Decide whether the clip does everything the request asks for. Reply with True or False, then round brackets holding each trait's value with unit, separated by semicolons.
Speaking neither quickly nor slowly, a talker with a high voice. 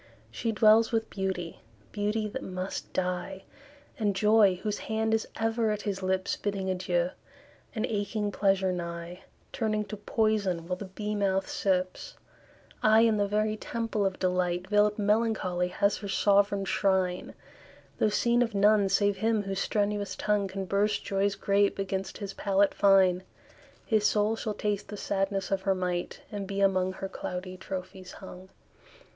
True (160 wpm; 200 Hz)